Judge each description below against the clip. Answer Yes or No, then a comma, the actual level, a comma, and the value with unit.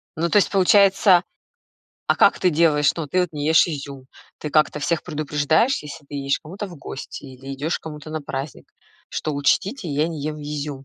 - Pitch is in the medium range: Yes, medium, 150 Hz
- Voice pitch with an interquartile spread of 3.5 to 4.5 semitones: No, average, 2.9 semitones